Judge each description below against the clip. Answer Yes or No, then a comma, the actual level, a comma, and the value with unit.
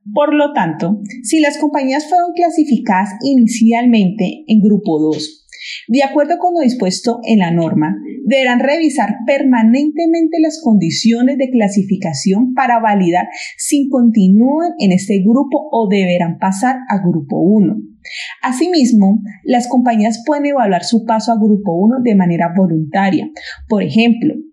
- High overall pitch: Yes, high, 230 Hz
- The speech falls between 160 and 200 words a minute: No, average, 135 wpm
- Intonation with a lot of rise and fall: Yes, wide, 5.7 semitones